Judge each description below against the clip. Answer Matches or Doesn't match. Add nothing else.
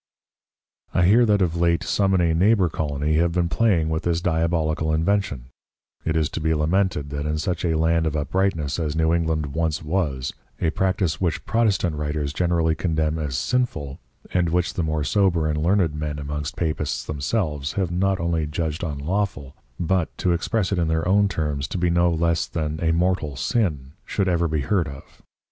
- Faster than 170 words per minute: Matches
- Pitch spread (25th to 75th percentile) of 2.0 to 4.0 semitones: Matches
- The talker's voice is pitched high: Doesn't match